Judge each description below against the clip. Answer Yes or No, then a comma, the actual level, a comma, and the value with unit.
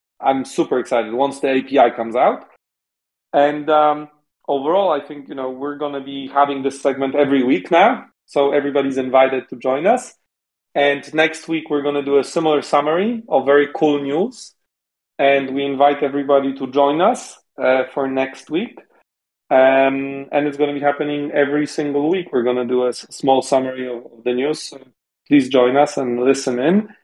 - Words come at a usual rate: Yes, average, 175 wpm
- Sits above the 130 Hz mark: Yes, medium, 140 Hz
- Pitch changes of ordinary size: No, narrow, 1.6 semitones